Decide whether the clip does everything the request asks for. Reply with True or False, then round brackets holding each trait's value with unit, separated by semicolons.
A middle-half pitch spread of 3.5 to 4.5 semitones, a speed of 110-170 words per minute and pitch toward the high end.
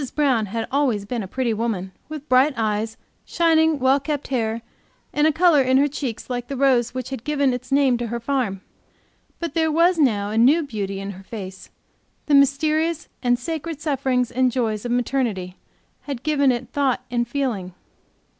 False (4.1 semitones; 185 wpm; 255 Hz)